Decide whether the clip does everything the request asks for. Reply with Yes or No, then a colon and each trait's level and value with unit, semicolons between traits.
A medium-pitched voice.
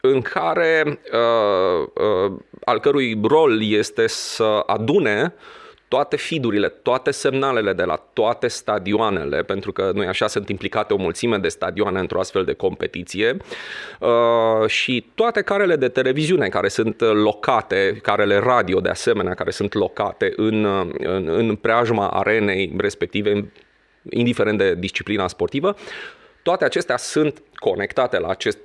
Yes: medium, 150 Hz